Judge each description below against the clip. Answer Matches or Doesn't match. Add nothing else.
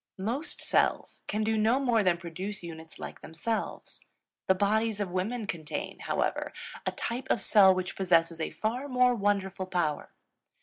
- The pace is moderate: Matches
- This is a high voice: Matches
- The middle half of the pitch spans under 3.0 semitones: Doesn't match